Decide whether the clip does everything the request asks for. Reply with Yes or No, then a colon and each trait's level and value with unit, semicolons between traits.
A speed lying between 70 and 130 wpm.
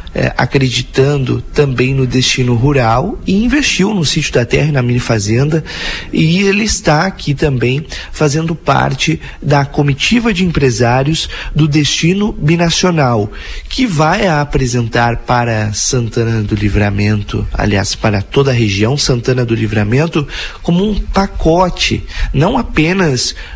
Yes: average, 125 wpm